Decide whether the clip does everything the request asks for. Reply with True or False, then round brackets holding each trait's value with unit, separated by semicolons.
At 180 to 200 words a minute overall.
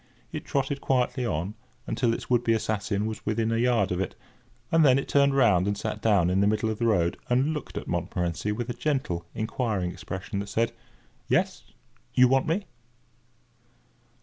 True (185 wpm)